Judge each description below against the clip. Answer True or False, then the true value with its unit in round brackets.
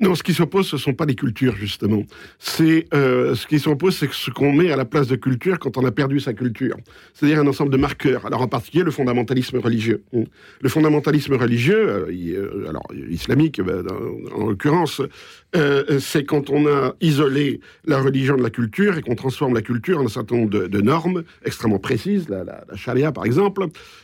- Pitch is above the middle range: False (140 Hz)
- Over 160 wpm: True (195 wpm)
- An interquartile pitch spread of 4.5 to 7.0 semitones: False (3.8 semitones)